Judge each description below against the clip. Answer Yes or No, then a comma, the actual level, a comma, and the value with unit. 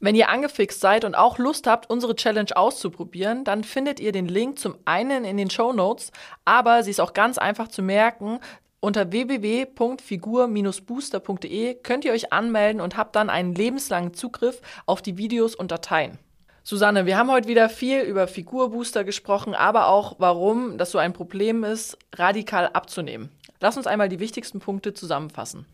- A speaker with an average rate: Yes, average, 170 wpm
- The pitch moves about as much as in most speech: Yes, average, 3.5 semitones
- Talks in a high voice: Yes, high, 215 Hz